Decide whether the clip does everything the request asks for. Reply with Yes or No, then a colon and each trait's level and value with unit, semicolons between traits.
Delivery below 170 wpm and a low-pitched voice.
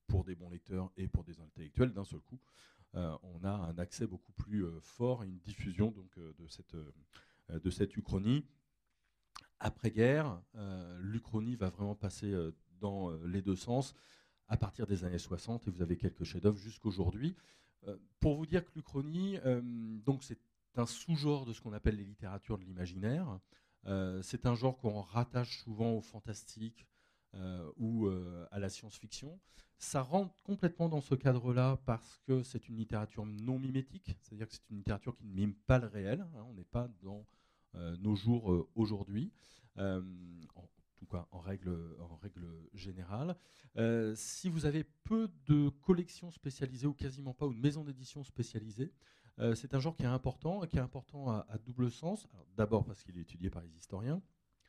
No: average, 190 wpm; low, 110 Hz